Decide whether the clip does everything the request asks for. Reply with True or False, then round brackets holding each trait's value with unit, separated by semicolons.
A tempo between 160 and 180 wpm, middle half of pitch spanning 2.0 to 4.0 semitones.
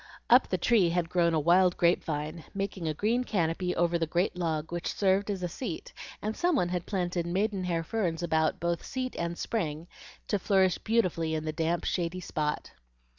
False (190 wpm; 2.9 semitones)